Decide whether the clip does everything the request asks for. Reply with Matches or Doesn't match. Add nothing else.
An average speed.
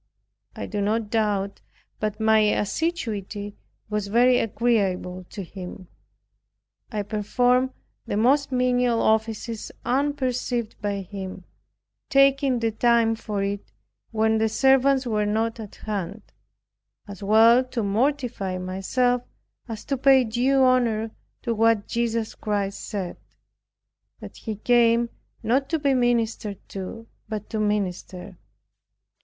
Doesn't match